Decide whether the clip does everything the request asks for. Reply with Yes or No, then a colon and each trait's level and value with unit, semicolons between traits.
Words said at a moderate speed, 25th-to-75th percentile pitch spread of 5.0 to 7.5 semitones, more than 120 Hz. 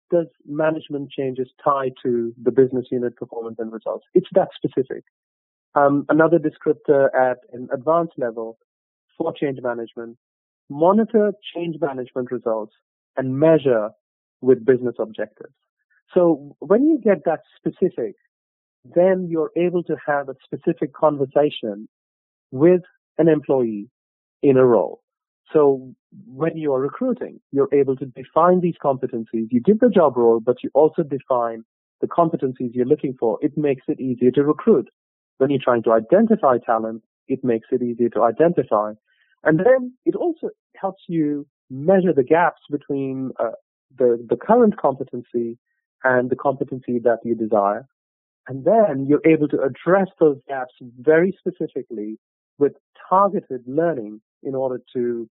Yes: average, 145 wpm; average, 5.3 semitones; medium, 140 Hz